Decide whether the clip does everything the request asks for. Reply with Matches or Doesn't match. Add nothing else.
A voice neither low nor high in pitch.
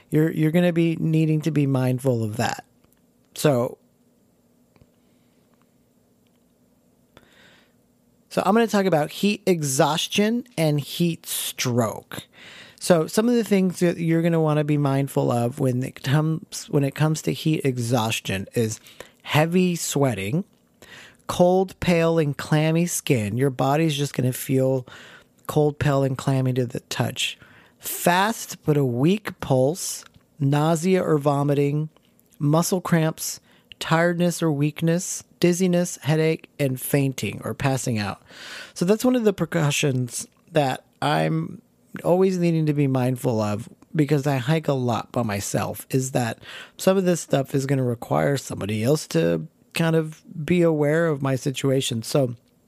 Matches